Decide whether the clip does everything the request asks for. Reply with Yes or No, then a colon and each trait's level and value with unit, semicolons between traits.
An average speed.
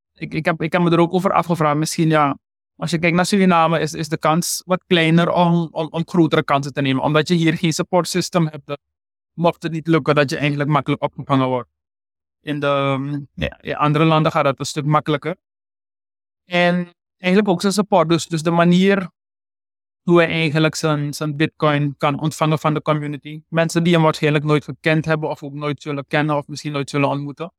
No: fast, 205 wpm